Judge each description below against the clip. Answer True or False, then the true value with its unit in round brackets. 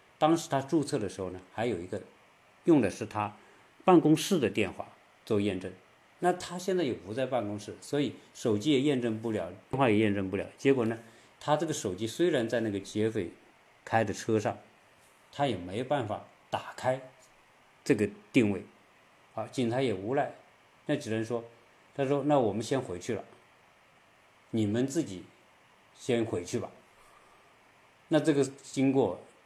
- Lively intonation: False (5.0 semitones)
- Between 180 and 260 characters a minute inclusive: True (230 characters per minute)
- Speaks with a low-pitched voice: True (120 Hz)